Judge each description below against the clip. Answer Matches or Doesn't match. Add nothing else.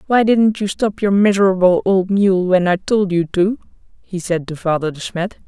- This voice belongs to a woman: Matches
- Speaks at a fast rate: Matches